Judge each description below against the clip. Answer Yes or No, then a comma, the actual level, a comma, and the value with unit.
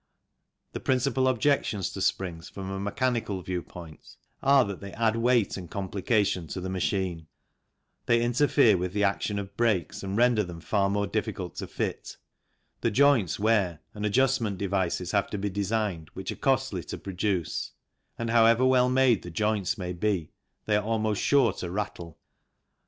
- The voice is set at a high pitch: No, low, 100 Hz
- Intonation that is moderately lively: Yes, average, 3.8 semitones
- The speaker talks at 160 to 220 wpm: Yes, average, 170 wpm